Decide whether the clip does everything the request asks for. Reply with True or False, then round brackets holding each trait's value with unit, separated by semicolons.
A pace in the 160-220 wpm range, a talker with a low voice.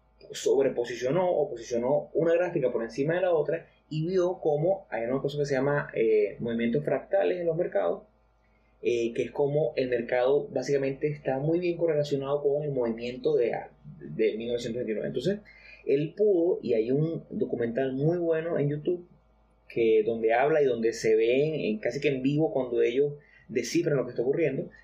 False (175 wpm; 145 Hz)